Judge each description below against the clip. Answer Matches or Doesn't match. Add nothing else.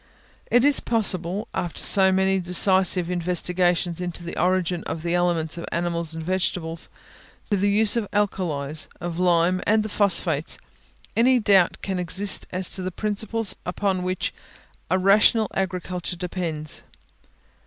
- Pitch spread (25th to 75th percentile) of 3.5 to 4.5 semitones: Doesn't match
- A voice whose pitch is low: Doesn't match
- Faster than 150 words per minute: Doesn't match